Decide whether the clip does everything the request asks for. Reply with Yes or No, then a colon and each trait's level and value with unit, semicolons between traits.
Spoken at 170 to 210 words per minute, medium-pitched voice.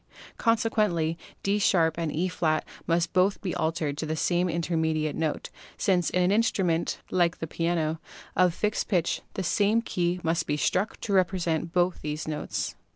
No: average, 160 wpm; medium, 170 Hz